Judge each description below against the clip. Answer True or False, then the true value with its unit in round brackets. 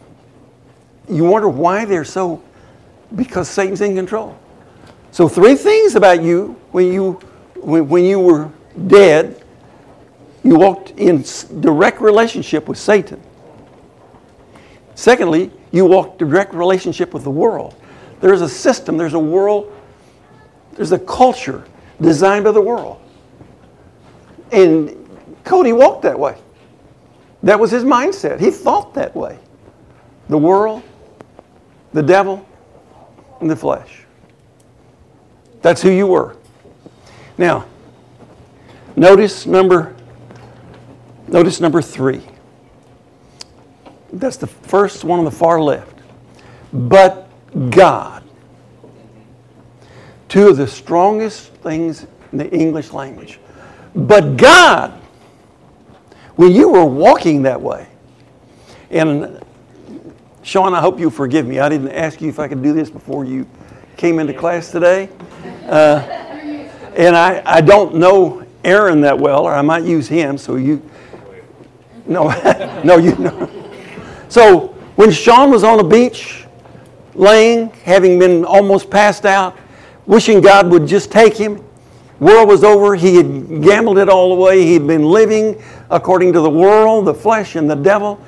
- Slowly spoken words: True (130 wpm)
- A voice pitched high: False (180 Hz)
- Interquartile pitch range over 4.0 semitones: True (4.5 semitones)